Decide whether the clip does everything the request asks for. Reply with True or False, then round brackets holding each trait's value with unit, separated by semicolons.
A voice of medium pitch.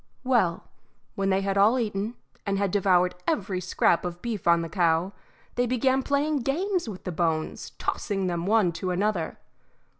False (195 Hz)